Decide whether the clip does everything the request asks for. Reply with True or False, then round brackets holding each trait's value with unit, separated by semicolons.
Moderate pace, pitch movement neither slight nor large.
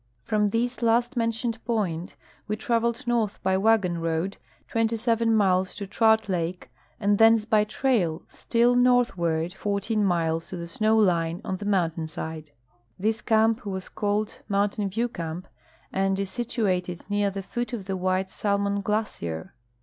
True (150 wpm; 3.6 semitones)